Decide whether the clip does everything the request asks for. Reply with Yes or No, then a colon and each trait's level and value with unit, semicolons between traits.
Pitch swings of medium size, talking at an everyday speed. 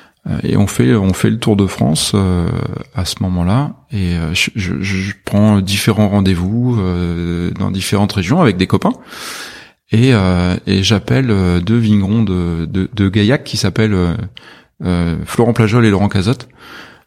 Yes: average, 3.2 semitones; average, 160 wpm